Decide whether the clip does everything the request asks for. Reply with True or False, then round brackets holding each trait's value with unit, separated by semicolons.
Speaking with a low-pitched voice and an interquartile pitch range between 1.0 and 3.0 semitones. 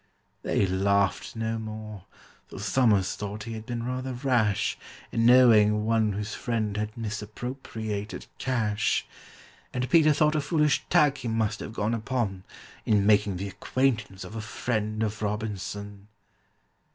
True (110 Hz; 2.7 semitones)